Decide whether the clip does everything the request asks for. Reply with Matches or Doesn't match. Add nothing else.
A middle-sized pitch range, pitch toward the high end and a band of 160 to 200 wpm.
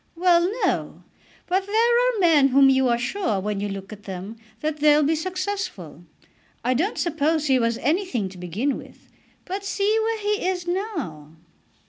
Doesn't match